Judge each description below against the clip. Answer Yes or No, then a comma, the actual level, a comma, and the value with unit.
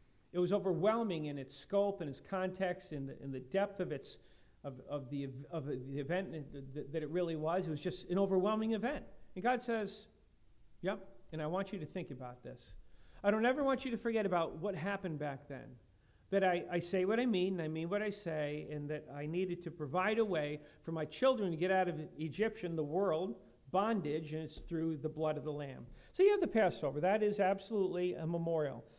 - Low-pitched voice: No, medium, 175 Hz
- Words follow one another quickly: Yes, fast, 225 wpm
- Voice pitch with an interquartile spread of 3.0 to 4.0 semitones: No, average, 4.8 semitones